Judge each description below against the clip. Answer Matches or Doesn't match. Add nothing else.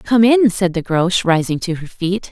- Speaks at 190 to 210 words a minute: Doesn't match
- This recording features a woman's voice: Matches